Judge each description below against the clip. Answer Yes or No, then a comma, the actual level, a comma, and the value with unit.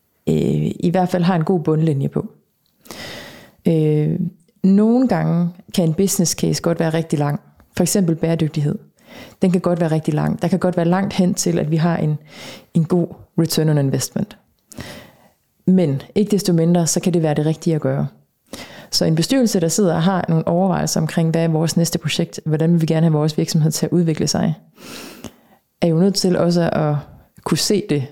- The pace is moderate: Yes, average, 195 wpm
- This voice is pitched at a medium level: Yes, medium, 170 Hz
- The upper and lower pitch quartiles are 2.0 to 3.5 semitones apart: Yes, narrow, 2.6 semitones